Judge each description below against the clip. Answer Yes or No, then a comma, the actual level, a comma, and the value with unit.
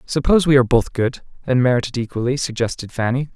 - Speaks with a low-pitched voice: Yes, low, 125 Hz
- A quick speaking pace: No, average, 195 wpm